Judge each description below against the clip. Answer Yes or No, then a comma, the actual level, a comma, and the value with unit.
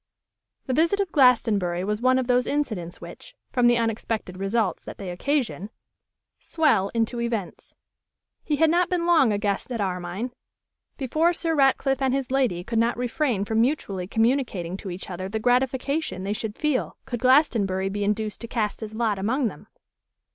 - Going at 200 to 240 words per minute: No, average, 175 wpm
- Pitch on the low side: No, high, 230 Hz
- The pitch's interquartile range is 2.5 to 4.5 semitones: No, average, 5.0 semitones